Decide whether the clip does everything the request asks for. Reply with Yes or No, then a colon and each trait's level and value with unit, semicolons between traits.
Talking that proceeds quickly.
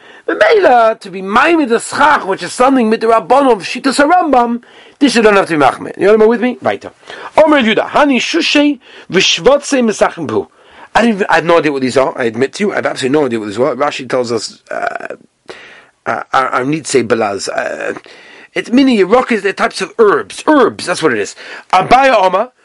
Yes: fast, 225 wpm